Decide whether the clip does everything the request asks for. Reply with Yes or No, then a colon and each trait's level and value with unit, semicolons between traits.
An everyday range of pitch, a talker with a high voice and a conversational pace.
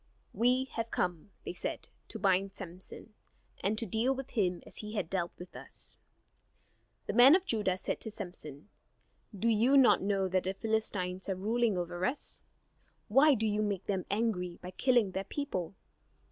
Yes: average, 3.8 semitones; high, 205 Hz; average, 175 wpm